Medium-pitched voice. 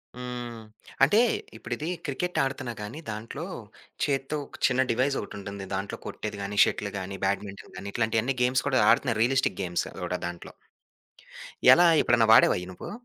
No: low, 120 Hz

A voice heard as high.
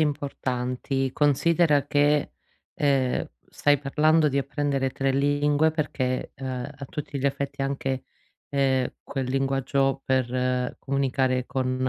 No: low, 135 Hz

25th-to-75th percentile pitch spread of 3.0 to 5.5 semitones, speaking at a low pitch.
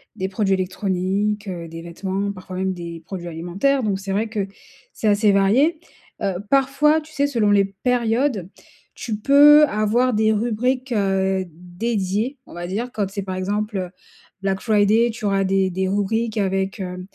No: average, 3.3 semitones; high, 200 Hz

